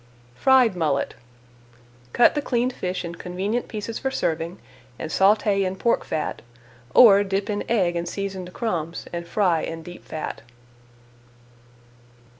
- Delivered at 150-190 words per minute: No, slow, 135 wpm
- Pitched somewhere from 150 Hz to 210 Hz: Yes, high, 190 Hz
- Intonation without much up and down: No, average, 4.2 semitones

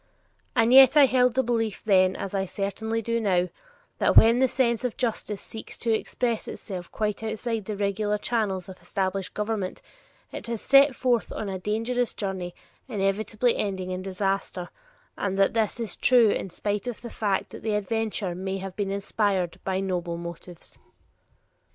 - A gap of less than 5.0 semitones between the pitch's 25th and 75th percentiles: Yes, average, 3.1 semitones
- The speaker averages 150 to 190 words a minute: Yes, average, 170 wpm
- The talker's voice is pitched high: Yes, high, 210 Hz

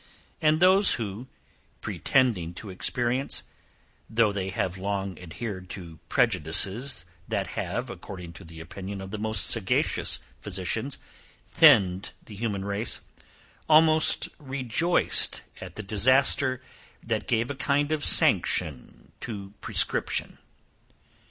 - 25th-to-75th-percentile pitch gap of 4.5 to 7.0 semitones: Yes, wide, 5.5 semitones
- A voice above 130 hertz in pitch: No, low, 110 Hz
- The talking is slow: Yes, slow, 115 wpm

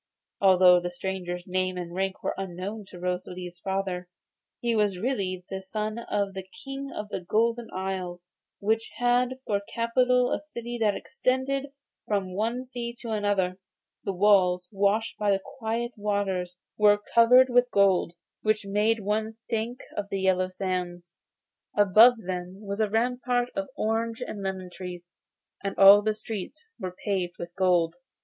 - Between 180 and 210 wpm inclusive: No, average, 155 wpm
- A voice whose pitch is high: Yes, high, 200 Hz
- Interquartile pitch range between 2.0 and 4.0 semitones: Yes, average, 3.6 semitones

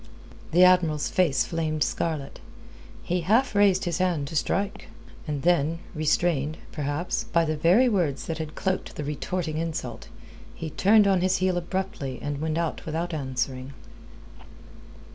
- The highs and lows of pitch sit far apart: No, average, 3.4 semitones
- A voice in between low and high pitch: Yes, medium, 165 Hz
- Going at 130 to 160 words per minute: Yes, average, 145 wpm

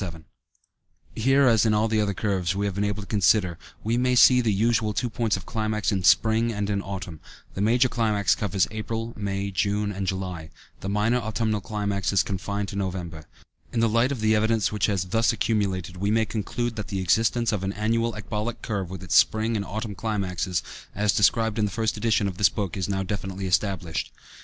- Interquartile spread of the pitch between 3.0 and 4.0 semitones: No, narrow, 2.5 semitones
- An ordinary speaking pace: No, fast, 210 wpm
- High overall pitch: No, low, 105 Hz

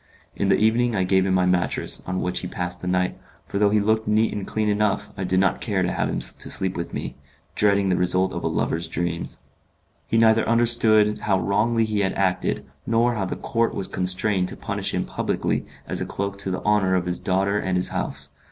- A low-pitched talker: Yes, low, 100 Hz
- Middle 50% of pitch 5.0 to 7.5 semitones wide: No, average, 2.7 semitones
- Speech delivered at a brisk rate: Yes, fast, 225 wpm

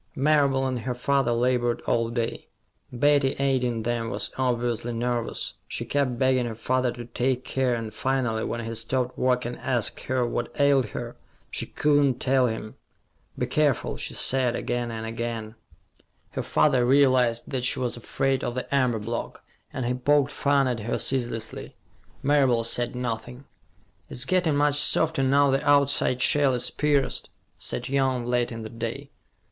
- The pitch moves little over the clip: Yes, narrow, 2.3 semitones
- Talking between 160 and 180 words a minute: Yes, average, 165 wpm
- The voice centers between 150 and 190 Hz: No, low, 125 Hz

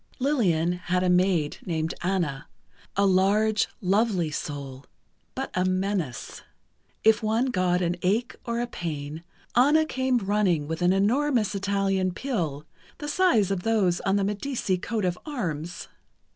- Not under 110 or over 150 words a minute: Yes, average, 145 wpm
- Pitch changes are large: No, average, 4.3 semitones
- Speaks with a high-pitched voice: Yes, high, 195 Hz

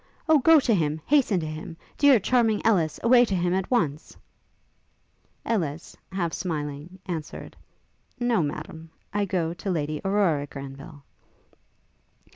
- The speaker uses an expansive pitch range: Yes, wide, 6.0 semitones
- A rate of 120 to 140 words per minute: Yes, slow, 135 wpm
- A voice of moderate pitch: Yes, medium, 175 Hz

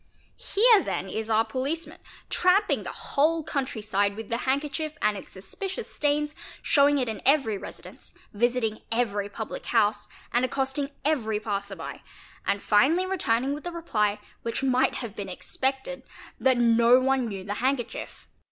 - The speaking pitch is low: No, very high, 250 Hz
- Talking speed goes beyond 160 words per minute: No, average, 155 wpm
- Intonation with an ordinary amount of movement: Yes, average, 5.0 semitones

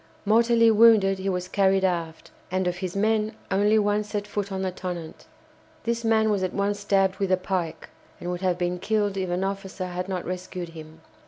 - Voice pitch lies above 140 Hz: Yes, high, 190 Hz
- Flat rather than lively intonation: Yes, narrow, 2.3 semitones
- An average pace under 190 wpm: No, average, 200 wpm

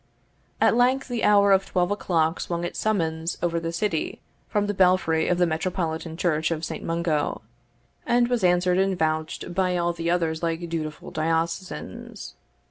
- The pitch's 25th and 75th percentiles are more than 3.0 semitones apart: No, average, 2.7 semitones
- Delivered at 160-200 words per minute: Yes, average, 165 wpm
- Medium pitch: Yes, medium, 175 Hz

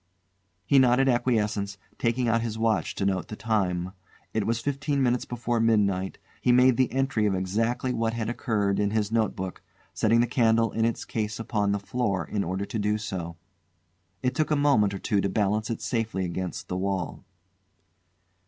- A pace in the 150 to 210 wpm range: Yes, average, 180 wpm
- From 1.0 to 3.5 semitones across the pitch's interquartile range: Yes, average, 3.2 semitones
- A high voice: No, low, 110 Hz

